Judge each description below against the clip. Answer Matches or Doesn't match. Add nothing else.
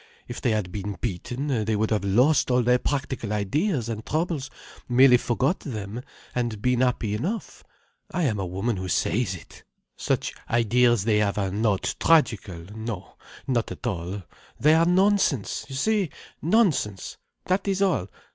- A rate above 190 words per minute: Doesn't match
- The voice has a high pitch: Doesn't match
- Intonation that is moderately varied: Doesn't match